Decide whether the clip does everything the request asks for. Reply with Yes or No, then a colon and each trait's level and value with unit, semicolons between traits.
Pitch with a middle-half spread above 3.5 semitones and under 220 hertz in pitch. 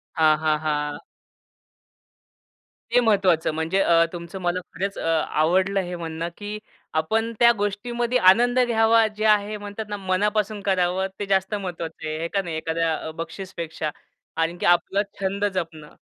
Yes: average, 3.9 semitones; medium, 185 Hz